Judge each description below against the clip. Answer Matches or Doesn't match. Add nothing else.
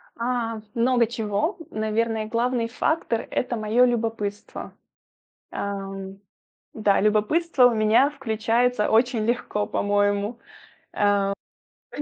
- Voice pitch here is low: Doesn't match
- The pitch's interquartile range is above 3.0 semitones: Doesn't match